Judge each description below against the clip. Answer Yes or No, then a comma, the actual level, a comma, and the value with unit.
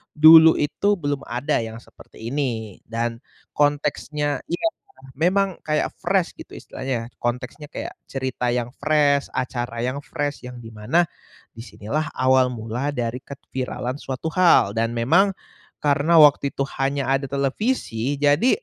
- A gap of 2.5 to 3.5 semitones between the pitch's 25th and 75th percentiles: No, average, 3.9 semitones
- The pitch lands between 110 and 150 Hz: Yes, medium, 140 Hz